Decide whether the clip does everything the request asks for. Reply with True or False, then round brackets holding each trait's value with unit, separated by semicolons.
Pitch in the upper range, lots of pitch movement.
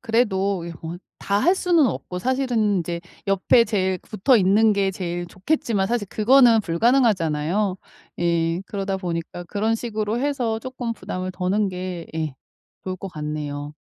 False (195 Hz; 4.5 semitones)